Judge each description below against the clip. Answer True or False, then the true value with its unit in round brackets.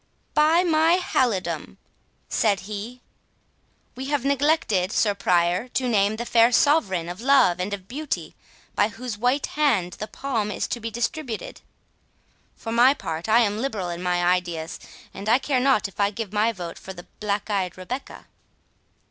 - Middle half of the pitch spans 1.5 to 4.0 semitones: False (5.4 semitones)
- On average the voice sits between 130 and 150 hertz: False (220 Hz)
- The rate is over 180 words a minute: False (165 wpm)